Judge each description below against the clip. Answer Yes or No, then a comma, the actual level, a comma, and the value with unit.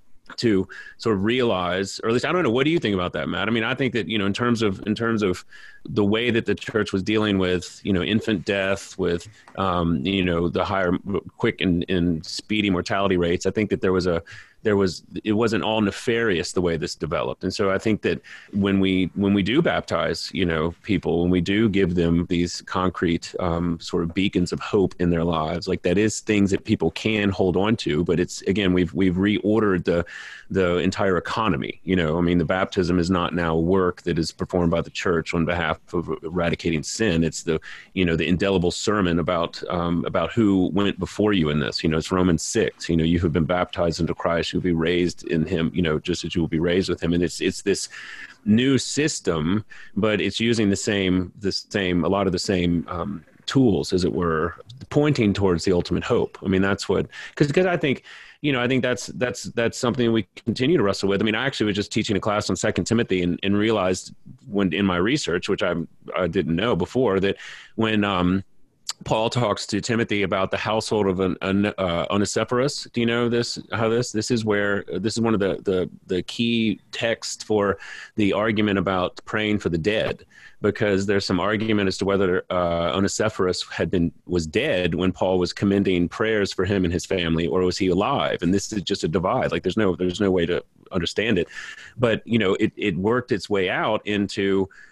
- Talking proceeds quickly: Yes, fast, 225 wpm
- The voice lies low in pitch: Yes, very low, 95 Hz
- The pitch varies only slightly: No, average, 3.4 semitones